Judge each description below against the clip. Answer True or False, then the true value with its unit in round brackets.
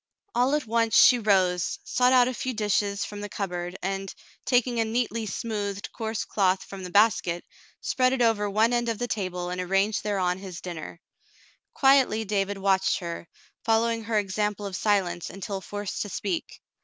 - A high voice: True (205 Hz)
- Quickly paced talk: False (175 wpm)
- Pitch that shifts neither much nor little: True (3.2 semitones)